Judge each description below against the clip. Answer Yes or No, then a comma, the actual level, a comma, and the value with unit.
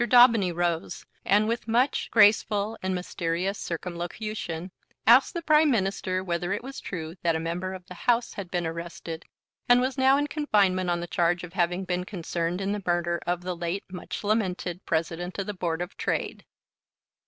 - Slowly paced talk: No, average, 180 wpm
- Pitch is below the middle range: No, medium, 185 Hz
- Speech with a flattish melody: No, average, 3.7 semitones